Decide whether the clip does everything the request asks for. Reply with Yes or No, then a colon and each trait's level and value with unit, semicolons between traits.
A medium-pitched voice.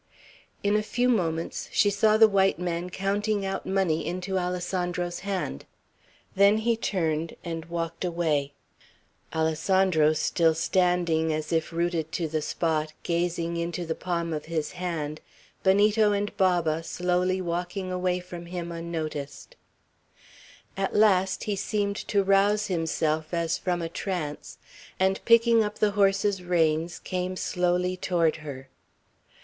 Yes: medium, 180 Hz